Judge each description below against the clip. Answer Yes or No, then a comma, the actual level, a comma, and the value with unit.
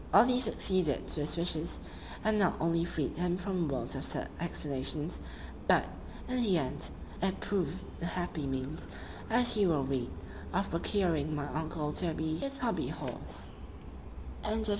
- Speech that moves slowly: No, average, 155 wpm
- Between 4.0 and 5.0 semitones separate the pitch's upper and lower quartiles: Yes, average, 4.4 semitones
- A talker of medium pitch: Yes, medium, 170 Hz